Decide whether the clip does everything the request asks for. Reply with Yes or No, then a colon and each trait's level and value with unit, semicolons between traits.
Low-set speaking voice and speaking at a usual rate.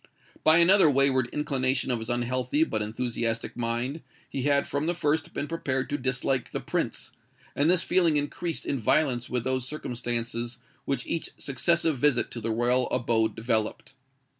Yes: low, 130 Hz; average, 165 wpm